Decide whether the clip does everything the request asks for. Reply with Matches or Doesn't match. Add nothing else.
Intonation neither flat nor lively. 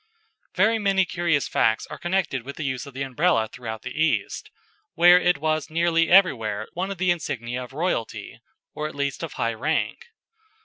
Doesn't match